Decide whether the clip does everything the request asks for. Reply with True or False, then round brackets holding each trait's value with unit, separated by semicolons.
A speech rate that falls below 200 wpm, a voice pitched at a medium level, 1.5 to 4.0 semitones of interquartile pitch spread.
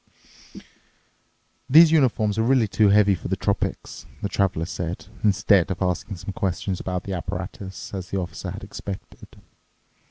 False (150 wpm; 100 Hz; 2.4 semitones)